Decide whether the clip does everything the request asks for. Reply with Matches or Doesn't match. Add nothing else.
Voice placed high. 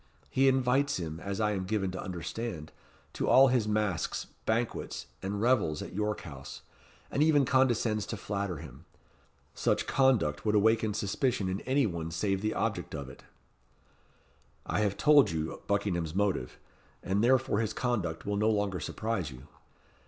Doesn't match